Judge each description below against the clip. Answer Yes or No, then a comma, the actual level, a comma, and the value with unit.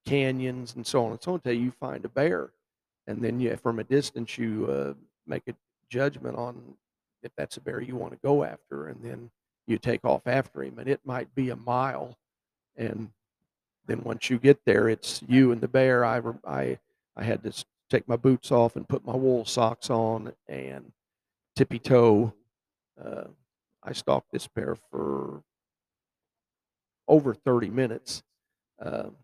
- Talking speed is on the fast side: No, average, 175 wpm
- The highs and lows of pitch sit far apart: No, narrow, 2.6 semitones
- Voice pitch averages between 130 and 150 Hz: No, low, 120 Hz